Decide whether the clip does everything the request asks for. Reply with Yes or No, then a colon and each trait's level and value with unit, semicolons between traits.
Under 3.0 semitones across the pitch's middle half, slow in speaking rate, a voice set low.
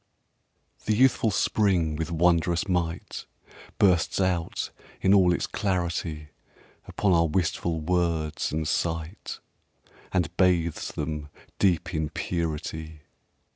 Yes: narrow, 2.4 semitones; slow, 110 wpm; very low, 85 Hz